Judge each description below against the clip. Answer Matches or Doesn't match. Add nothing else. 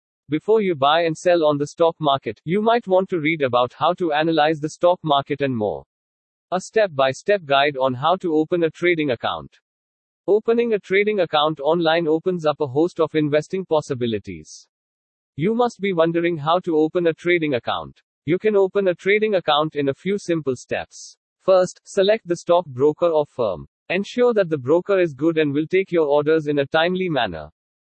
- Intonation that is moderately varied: Matches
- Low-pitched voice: Doesn't match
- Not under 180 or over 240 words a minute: Matches